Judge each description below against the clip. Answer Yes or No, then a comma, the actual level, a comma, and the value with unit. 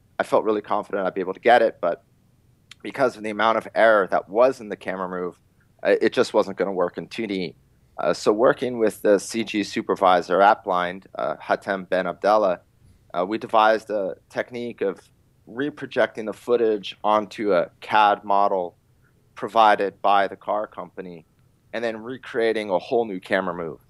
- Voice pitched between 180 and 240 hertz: No, low, 110 Hz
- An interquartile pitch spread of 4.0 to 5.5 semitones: No, average, 3.3 semitones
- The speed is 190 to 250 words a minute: No, average, 175 wpm